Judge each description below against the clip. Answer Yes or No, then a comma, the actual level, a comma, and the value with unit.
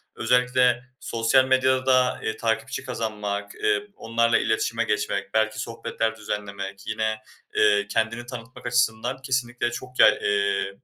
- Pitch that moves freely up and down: No, average, 2.9 semitones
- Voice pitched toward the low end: Yes, low, 115 Hz